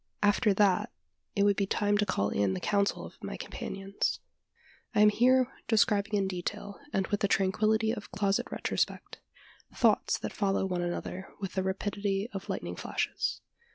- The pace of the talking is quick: No, average, 165 wpm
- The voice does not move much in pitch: Yes, narrow, 1.5 semitones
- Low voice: No, high, 200 Hz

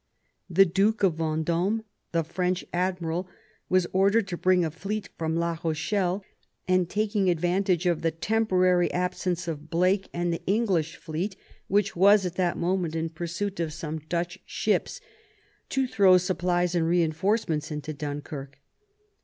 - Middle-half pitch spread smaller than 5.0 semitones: Yes, average, 2.7 semitones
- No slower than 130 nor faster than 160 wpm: Yes, average, 145 wpm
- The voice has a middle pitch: Yes, medium, 180 Hz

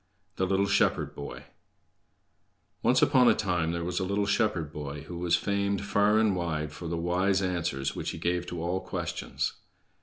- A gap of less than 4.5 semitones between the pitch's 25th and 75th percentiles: Yes, average, 3.1 semitones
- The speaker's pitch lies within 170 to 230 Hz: No, very low, 90 Hz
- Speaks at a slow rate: No, average, 180 wpm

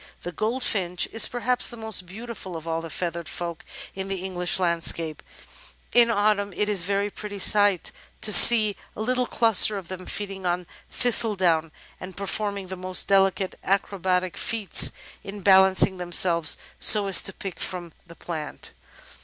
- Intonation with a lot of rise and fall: No, average, 2.8 semitones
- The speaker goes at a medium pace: Yes, average, 160 wpm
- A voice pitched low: No, high, 190 Hz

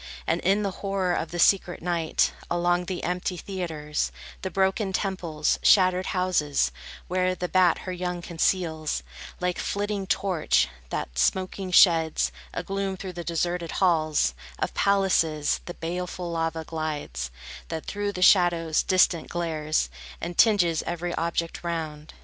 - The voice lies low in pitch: No, medium, 175 Hz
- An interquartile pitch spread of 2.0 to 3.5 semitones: Yes, narrow, 2.4 semitones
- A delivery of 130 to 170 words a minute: Yes, average, 140 wpm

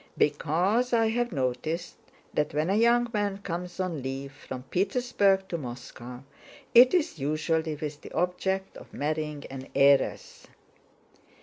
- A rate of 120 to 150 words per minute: Yes, slow, 135 wpm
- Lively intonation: Yes, wide, 5.7 semitones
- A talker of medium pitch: Yes, medium, 165 Hz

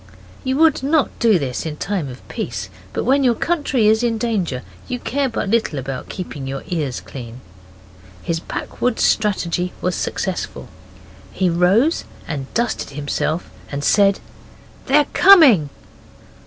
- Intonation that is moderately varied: No, wide, 8.7 semitones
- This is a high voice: Yes, high, 195 Hz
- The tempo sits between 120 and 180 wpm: Yes, average, 140 wpm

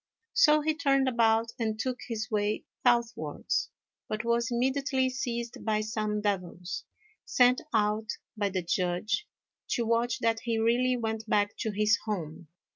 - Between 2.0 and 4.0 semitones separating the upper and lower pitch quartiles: Yes, narrow, 2.6 semitones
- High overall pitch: Yes, high, 225 Hz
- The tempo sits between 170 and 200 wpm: No, average, 145 wpm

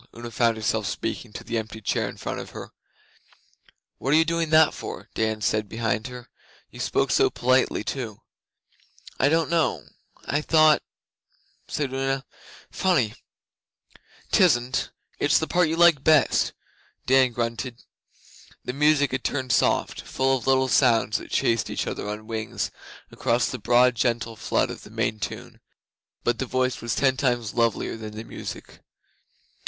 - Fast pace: No, average, 160 wpm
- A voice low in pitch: Yes, low, 125 Hz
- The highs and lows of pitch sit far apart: No, average, 3.6 semitones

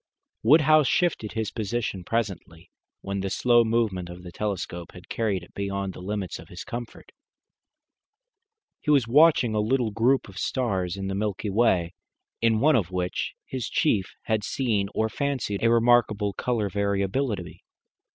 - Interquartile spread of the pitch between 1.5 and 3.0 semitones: No, average, 3.7 semitones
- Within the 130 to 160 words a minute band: Yes, average, 155 wpm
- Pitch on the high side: No, low, 105 Hz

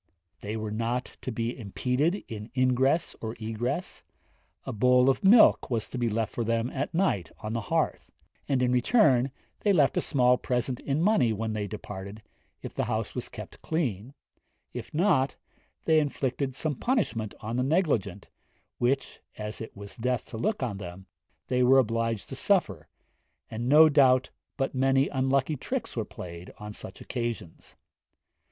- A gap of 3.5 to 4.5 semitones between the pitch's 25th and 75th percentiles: Yes, average, 3.8 semitones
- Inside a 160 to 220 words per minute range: Yes, average, 165 wpm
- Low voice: Yes, low, 125 Hz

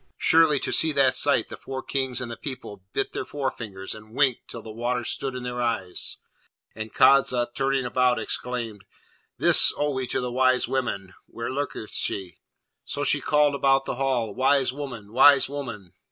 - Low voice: Yes, low, 125 Hz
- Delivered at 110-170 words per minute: No, average, 180 wpm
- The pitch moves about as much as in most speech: Yes, average, 3.0 semitones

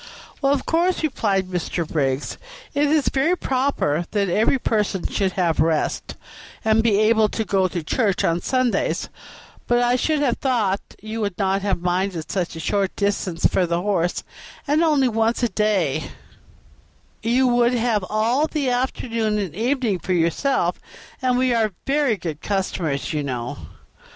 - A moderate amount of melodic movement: No, wide, 5.7 semitones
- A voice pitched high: Yes, high, 215 Hz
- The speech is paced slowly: No, average, 160 wpm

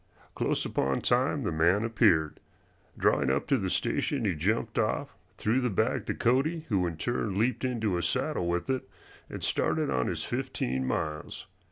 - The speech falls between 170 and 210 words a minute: Yes, average, 175 wpm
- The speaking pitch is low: Yes, low, 100 Hz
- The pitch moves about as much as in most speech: No, wide, 7.4 semitones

